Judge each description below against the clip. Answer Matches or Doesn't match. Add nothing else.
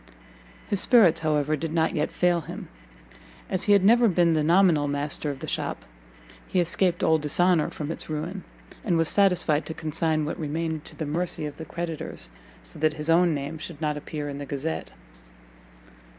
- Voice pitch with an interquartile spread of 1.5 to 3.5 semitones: Matches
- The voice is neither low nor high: Matches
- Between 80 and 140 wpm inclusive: Doesn't match